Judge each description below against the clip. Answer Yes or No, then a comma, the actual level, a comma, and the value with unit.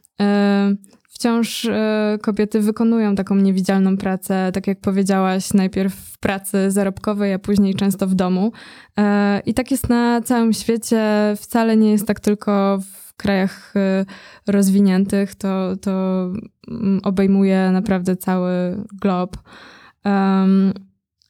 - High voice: Yes, high, 200 Hz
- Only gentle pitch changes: Yes, narrow, 1.6 semitones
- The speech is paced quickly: No, slow, 110 wpm